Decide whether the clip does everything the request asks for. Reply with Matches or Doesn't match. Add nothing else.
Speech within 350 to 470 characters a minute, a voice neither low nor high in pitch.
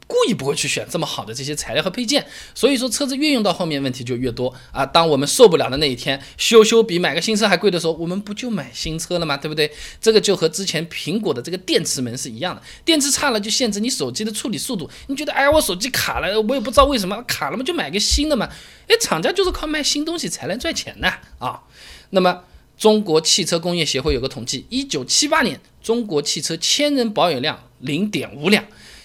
Doesn't match